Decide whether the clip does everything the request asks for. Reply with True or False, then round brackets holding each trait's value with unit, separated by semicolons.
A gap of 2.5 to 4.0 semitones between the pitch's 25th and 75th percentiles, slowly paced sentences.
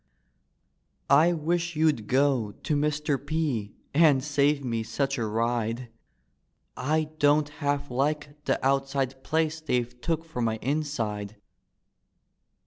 True (3.6 semitones; 125 wpm)